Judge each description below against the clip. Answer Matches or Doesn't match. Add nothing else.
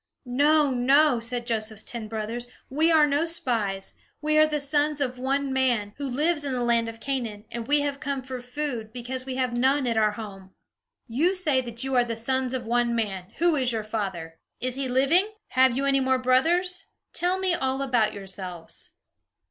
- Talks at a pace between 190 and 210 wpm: Matches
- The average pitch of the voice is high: Matches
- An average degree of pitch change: Matches